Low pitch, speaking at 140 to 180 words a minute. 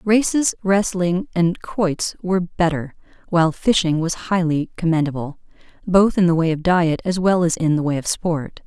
No: medium, 175 Hz; average, 175 wpm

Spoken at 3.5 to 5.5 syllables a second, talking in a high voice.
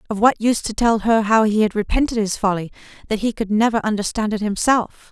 No: 6.1 syllables/s; high, 215 Hz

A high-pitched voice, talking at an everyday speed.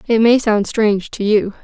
No: high, 215 Hz; fast, 220 wpm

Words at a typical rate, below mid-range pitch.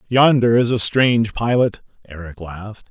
Yes: average, 145 wpm; low, 110 Hz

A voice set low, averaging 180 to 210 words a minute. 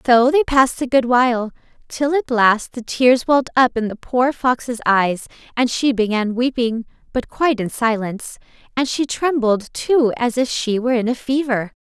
No: high, 245 Hz; average, 190 wpm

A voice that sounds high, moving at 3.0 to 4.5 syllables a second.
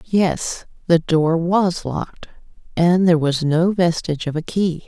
No: medium, 170 Hz; 4.2 syllables/s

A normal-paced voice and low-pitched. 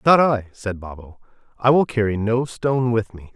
Yes: average, 195 wpm; low, 115 Hz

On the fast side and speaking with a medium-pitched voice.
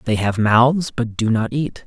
No: fast, 225 wpm; low, 120 Hz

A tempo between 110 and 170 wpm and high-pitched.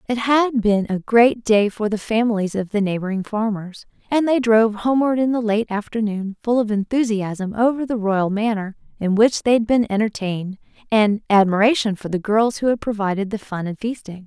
No: average, 195 wpm; high, 215 Hz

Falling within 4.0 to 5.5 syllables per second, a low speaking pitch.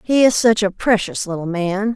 No: 4.9 syllables/s; high, 205 Hz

